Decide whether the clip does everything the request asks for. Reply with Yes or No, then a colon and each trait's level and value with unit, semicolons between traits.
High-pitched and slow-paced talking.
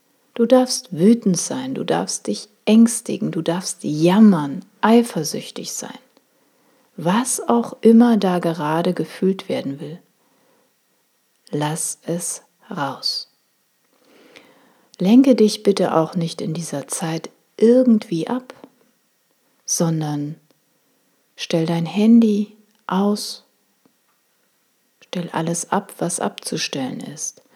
Yes: high, 210 Hz; slow, 100 wpm